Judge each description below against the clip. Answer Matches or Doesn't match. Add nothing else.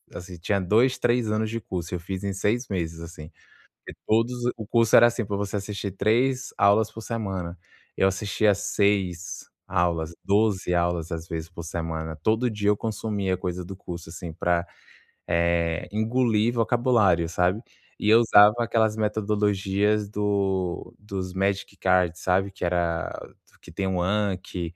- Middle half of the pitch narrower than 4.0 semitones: Matches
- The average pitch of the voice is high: Doesn't match